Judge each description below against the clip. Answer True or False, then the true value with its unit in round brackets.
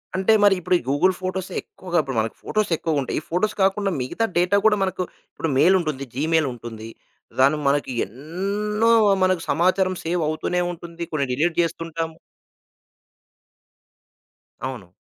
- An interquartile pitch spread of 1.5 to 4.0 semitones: False (4.4 semitones)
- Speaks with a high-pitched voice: False (170 Hz)